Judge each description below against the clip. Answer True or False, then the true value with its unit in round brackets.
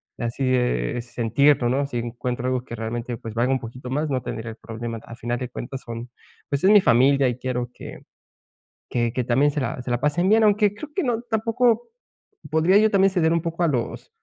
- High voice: False (130 Hz)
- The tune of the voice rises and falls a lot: True (6.1 semitones)